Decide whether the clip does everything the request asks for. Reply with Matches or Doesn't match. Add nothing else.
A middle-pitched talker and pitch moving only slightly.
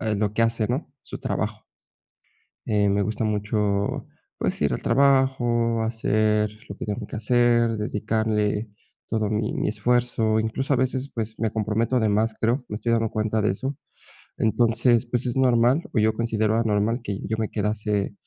Doesn't match